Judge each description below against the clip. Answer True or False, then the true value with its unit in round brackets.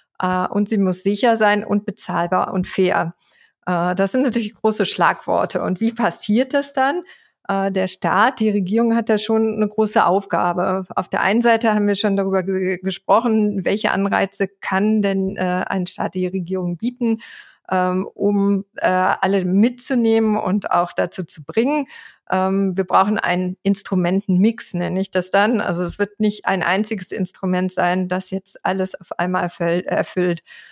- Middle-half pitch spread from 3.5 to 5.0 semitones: False (2.8 semitones)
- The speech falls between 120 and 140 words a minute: False (170 wpm)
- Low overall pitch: False (195 Hz)